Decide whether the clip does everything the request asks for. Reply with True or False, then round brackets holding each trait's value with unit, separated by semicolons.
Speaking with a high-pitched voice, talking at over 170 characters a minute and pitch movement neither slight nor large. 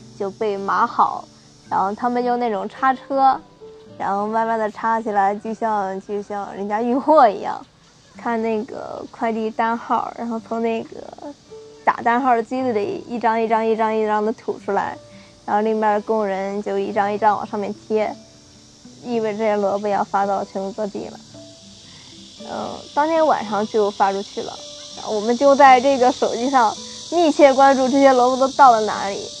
True (220 Hz; 260 characters per minute; 3.3 semitones)